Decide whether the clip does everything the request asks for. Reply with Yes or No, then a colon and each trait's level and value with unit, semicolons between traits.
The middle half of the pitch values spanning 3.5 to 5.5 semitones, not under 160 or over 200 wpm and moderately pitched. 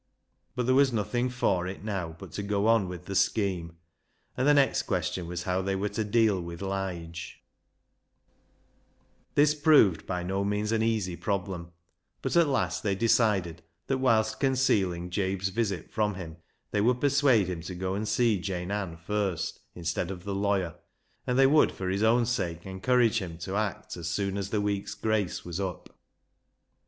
No: average, 3.8 semitones; average, 180 wpm; low, 100 Hz